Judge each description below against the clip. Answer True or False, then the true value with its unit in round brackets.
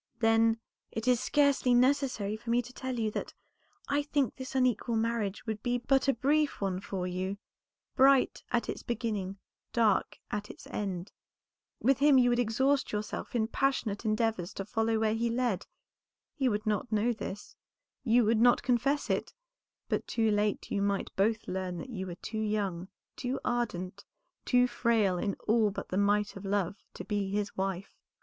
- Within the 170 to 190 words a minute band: True (175 wpm)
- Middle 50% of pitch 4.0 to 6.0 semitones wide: False (3.5 semitones)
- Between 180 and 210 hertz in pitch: False (225 Hz)